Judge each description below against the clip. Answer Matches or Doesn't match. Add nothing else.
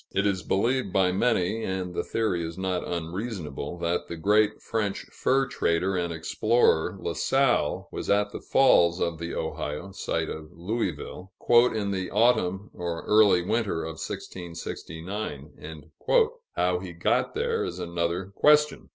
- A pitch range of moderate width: Matches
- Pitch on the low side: Matches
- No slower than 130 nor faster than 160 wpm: Matches